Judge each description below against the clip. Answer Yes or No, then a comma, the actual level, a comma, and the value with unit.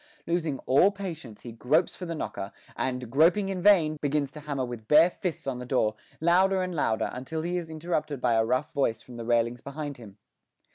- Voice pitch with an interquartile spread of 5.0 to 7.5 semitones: Yes, wide, 5.4 semitones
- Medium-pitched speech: Yes, medium, 145 Hz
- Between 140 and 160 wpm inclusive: No, fast, 205 wpm